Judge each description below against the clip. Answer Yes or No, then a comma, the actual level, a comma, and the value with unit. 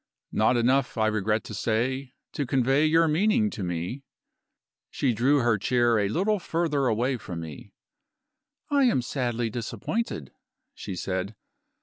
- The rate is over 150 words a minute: No, average, 140 wpm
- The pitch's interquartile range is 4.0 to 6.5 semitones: Yes, average, 5.0 semitones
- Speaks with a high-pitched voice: No, low, 120 Hz